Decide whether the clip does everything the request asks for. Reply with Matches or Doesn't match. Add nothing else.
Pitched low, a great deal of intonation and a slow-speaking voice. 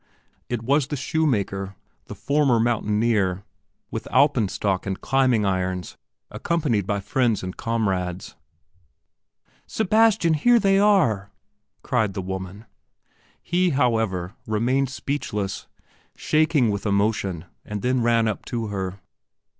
Matches